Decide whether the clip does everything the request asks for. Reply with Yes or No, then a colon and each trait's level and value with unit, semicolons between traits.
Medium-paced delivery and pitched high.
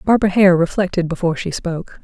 No: average, 175 wpm; medium, 180 Hz